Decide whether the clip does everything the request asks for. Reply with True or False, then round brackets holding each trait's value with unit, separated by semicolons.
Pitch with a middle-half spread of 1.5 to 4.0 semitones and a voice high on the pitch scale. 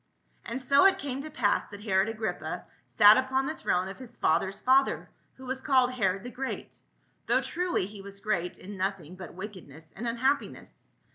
False (5.4 semitones; 220 Hz)